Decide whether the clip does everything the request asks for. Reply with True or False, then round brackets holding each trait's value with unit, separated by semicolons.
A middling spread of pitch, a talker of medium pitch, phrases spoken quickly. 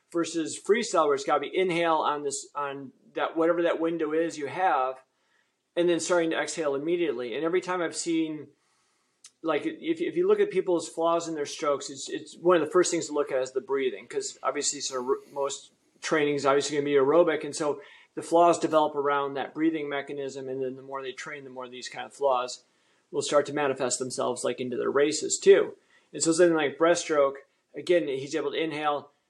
True (4.3 semitones; 160 Hz; 215 wpm)